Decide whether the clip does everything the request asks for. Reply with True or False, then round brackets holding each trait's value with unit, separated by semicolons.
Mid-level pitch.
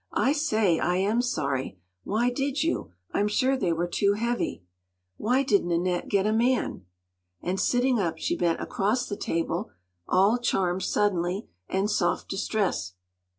False (205 Hz)